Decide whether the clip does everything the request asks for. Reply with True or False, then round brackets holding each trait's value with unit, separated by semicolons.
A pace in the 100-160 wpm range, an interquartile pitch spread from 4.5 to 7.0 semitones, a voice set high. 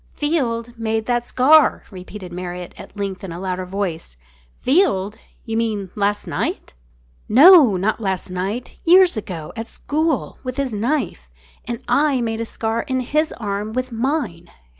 True (155 wpm; 5.1 semitones; 225 Hz)